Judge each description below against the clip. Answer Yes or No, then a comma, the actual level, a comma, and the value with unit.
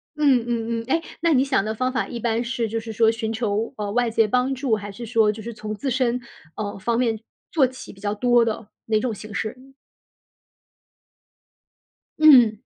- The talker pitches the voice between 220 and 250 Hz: Yes, high, 230 Hz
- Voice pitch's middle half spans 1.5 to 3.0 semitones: Yes, average, 2.7 semitones